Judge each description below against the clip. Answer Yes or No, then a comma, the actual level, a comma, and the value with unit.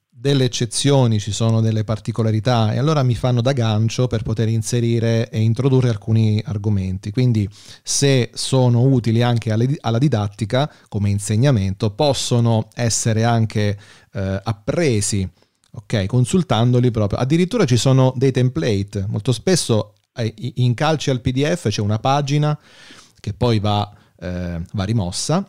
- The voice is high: No, low, 115 Hz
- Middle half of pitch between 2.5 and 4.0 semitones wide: Yes, average, 3.3 semitones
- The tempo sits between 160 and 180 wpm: No, average, 130 wpm